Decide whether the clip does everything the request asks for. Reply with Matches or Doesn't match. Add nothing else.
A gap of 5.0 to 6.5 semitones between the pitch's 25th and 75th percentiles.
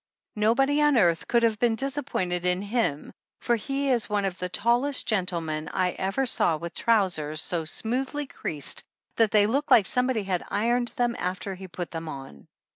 Matches